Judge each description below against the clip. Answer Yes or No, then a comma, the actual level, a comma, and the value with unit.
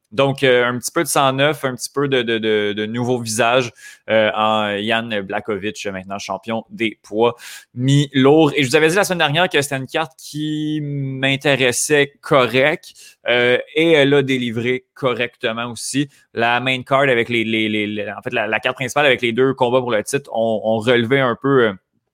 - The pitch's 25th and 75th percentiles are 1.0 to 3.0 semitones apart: No, average, 3.7 semitones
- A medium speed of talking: Yes, average, 200 wpm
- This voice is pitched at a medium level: No, low, 125 Hz